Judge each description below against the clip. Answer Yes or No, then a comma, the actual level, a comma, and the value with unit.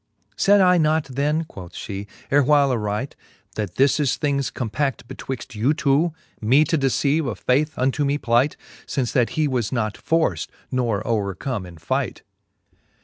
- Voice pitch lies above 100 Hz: Yes, low, 135 Hz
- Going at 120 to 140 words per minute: No, average, 155 wpm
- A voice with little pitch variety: No, average, 4.3 semitones